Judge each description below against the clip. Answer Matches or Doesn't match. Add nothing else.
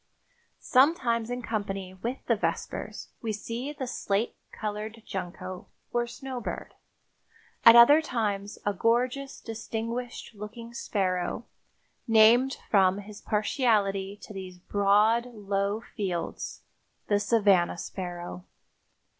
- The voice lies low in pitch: Doesn't match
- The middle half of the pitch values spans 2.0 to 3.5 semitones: Matches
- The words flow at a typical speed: Doesn't match